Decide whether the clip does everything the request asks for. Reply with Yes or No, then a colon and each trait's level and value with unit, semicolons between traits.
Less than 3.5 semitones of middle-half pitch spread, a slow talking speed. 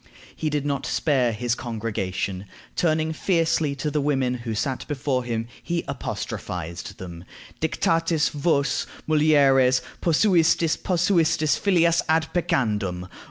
No: average, 5.3 semitones; slow, 115 wpm